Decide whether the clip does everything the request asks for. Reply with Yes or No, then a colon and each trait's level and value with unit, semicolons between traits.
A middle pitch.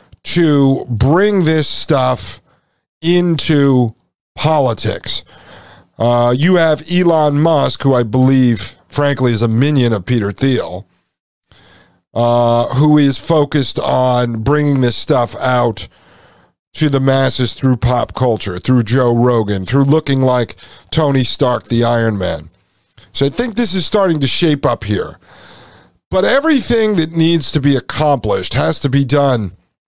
No: low, 130 Hz